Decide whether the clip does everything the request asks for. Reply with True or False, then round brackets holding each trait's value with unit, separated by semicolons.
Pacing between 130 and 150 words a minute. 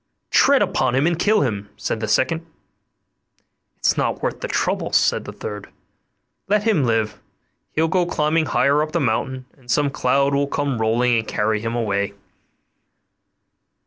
False (160 wpm)